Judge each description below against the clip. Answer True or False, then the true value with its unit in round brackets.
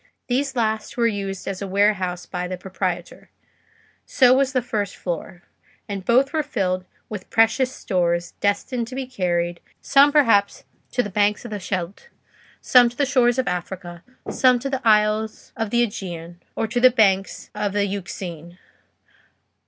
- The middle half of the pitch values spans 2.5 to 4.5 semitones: False (4.9 semitones)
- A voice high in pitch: True (205 Hz)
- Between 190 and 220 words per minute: False (165 wpm)